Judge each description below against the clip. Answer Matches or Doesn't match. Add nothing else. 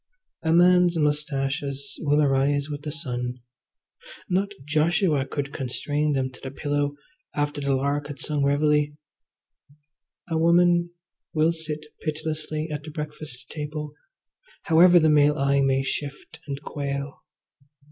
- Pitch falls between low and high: Matches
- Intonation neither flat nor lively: Doesn't match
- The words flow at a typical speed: Doesn't match